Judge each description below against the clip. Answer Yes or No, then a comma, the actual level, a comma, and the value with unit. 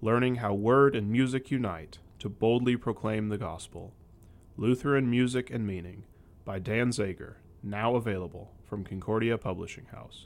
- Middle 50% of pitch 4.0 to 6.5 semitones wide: Yes, average, 4.5 semitones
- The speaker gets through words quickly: No, average, 140 wpm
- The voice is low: Yes, low, 105 Hz